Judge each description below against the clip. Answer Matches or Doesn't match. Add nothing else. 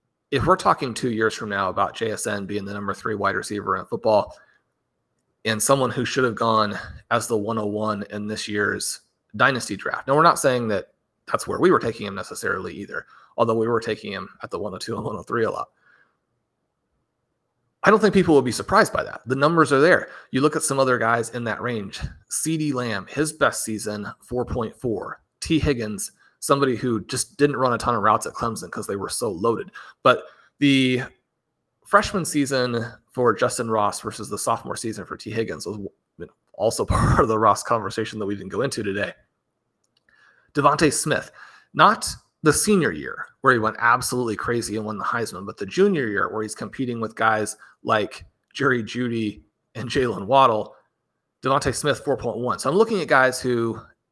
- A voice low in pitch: Matches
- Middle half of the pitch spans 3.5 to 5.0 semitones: Matches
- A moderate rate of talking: Matches